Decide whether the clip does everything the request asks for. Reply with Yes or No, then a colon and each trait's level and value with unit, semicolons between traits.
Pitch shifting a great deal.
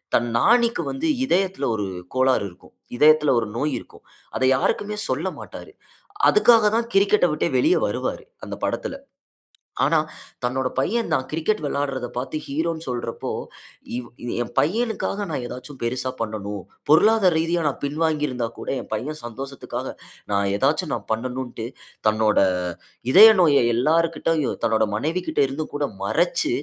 Yes: wide, 5.9 semitones